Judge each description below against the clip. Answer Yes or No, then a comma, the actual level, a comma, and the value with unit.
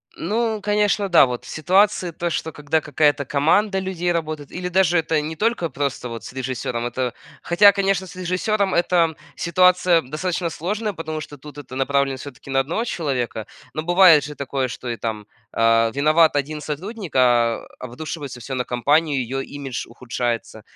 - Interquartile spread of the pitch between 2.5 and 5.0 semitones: No, wide, 5.4 semitones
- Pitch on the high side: No, medium, 155 Hz